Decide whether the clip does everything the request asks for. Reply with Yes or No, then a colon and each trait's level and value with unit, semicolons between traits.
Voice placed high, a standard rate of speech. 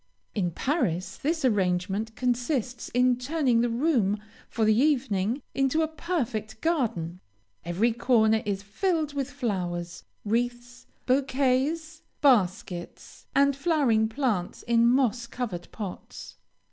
No: high, 240 Hz; slow, 115 wpm